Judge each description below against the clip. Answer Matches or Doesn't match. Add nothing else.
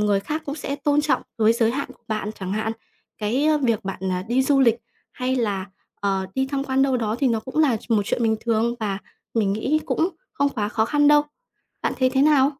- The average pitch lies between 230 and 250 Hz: Matches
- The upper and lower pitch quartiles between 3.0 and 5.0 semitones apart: Matches